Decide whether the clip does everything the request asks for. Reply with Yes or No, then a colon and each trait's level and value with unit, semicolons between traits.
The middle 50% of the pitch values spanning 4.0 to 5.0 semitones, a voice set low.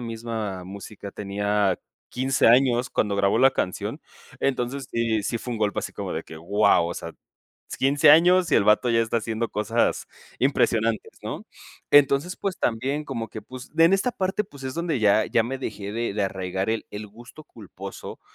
Yes: average, 4.5 semitones; low, 115 Hz